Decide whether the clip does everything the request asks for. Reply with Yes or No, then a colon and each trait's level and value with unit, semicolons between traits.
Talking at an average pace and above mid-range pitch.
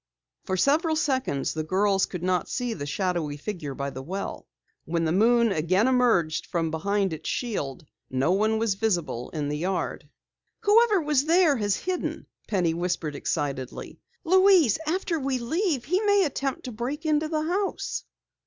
Yes: average, 160 wpm; high, 210 Hz